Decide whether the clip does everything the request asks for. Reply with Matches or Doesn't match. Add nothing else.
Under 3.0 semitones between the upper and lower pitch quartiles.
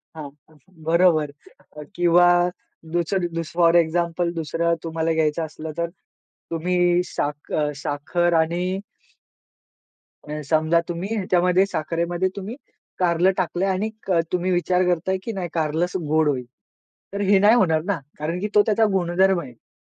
Matches